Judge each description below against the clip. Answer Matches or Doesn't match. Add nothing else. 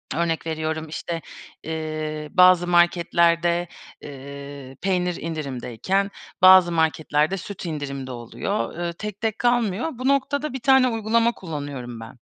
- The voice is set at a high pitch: Doesn't match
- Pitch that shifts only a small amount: Doesn't match